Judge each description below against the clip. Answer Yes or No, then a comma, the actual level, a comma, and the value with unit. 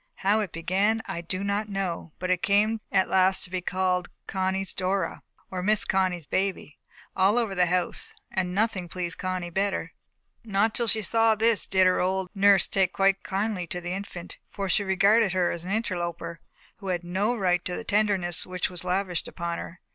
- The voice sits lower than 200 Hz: Yes, high, 190 Hz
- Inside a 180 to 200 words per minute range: Yes, average, 195 wpm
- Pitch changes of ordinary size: No, narrow, 2.0 semitones